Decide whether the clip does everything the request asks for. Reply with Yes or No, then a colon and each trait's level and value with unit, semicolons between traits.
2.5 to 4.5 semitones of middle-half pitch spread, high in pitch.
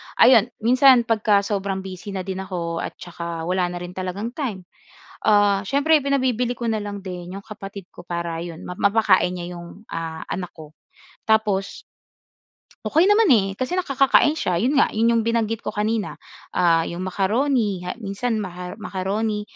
Yes: average, 4.2 semitones; high, 200 Hz